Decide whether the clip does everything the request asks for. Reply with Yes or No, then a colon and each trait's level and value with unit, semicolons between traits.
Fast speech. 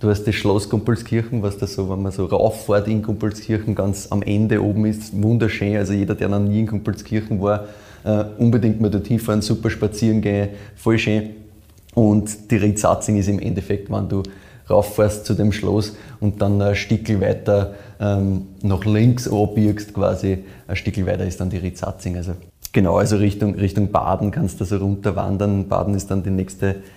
No: average, 180 wpm